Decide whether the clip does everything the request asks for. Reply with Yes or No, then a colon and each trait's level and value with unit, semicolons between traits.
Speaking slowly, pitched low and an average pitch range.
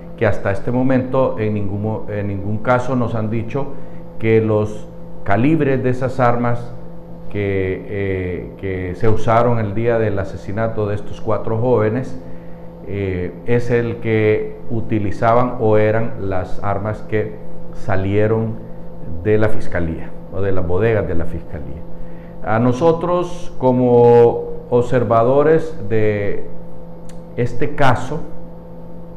Yes: slow, 120 wpm; low, 110 Hz; average, 4.2 semitones